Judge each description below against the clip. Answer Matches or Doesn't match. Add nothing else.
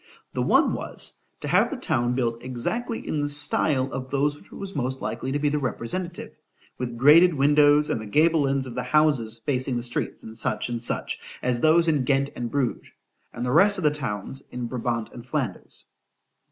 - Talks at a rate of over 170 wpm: Matches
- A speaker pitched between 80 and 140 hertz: Matches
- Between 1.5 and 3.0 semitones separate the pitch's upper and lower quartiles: Doesn't match